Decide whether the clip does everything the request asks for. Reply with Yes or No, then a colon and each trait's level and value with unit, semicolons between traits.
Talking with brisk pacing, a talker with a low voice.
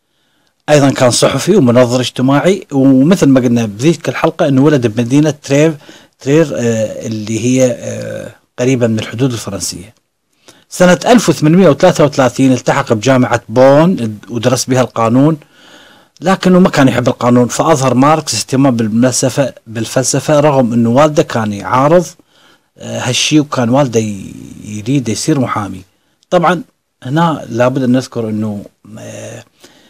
No: average, 110 wpm; low, 130 Hz